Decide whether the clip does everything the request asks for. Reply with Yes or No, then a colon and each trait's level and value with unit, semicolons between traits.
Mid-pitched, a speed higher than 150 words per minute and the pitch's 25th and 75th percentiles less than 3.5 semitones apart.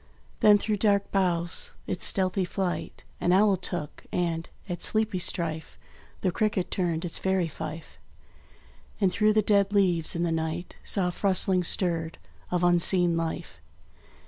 No: medium, 180 Hz; average, 145 wpm; narrow, 2.6 semitones